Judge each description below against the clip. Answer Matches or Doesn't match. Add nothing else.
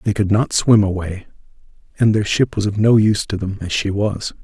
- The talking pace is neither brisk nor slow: Doesn't match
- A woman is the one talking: Doesn't match